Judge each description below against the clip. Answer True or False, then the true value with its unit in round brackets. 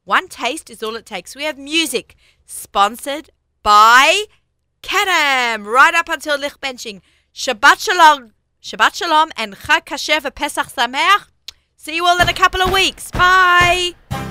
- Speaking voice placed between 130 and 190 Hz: False (305 Hz)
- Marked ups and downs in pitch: True (5.7 semitones)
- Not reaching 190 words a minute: True (140 wpm)